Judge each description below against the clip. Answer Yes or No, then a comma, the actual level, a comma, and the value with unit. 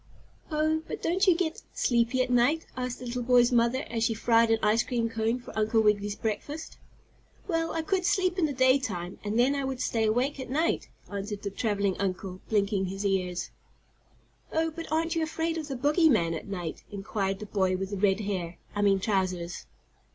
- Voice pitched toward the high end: Yes, high, 230 Hz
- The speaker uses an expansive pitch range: Yes, wide, 6.2 semitones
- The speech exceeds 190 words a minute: Yes, average, 200 wpm